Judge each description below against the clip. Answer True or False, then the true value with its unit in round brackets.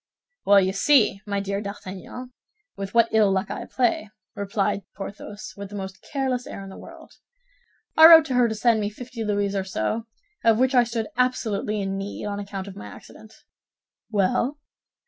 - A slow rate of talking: False (185 wpm)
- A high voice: True (205 Hz)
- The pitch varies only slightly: False (3.1 semitones)